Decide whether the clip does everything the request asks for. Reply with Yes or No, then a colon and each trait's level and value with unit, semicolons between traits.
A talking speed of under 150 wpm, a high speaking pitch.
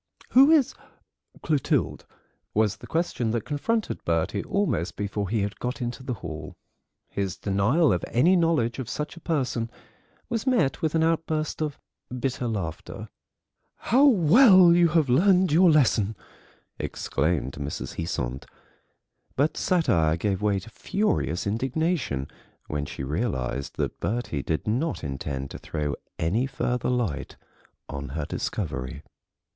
No: slow, 135 wpm; low, 120 Hz